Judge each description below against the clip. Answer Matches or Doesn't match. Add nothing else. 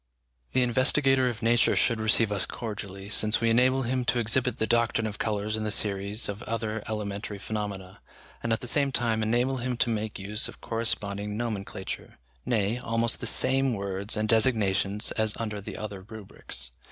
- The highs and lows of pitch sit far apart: Doesn't match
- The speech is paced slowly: Doesn't match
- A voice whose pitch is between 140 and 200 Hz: Doesn't match